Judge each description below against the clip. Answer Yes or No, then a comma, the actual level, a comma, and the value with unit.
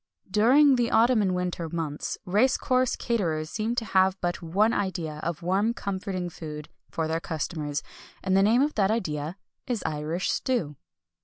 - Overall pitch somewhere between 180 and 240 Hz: Yes, medium, 185 Hz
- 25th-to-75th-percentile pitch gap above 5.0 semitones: Yes, wide, 5.6 semitones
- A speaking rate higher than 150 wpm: Yes, average, 165 wpm